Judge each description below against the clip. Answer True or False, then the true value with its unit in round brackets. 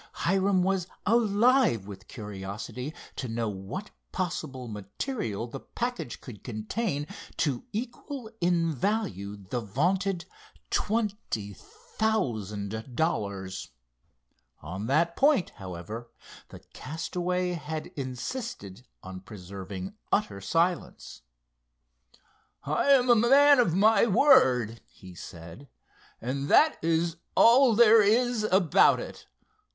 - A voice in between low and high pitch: True (155 Hz)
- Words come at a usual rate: False (105 wpm)